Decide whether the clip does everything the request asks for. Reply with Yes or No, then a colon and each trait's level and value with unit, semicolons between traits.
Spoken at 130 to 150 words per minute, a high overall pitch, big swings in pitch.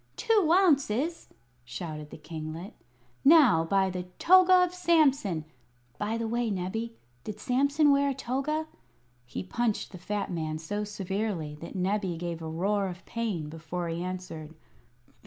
Yes: average, 145 wpm; high, 205 Hz; wide, 8.1 semitones